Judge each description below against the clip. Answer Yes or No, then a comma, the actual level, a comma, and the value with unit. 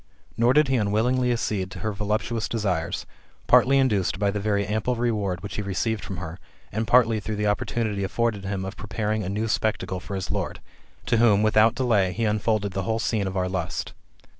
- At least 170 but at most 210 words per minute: Yes, average, 200 wpm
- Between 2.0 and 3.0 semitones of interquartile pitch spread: Yes, narrow, 2.5 semitones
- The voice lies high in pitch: No, low, 105 Hz